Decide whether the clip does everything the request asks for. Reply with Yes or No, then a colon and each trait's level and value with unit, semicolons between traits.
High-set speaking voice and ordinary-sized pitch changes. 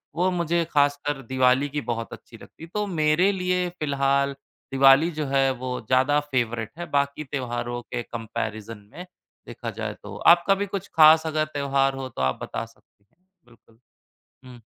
No: medium, 140 Hz; average, 4.4 semitones